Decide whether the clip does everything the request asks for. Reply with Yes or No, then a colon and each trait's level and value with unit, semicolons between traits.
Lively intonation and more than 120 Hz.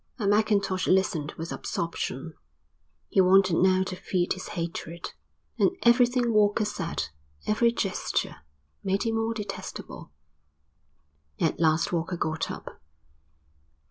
No: average, 4.0 semitones; high, 190 Hz